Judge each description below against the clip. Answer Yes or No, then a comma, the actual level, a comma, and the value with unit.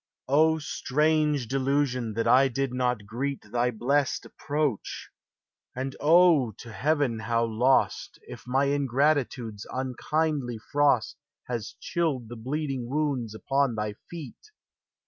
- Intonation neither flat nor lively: Yes, average, 3.5 semitones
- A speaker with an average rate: No, slow, 120 wpm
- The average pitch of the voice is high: No, low, 135 Hz